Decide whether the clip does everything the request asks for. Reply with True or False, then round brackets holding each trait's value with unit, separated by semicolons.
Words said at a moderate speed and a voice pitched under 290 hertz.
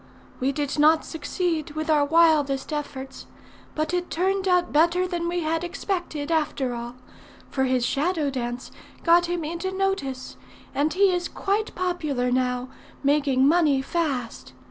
False (150 wpm; 310 Hz)